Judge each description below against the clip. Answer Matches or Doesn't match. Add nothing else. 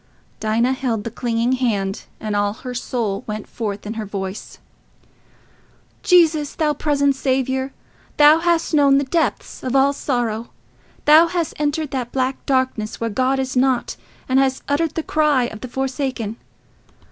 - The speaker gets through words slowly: Doesn't match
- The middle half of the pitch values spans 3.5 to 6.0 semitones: Matches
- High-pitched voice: Matches